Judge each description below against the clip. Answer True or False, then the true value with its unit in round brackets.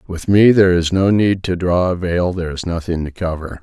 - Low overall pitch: True (90 Hz)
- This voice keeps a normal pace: False (250 wpm)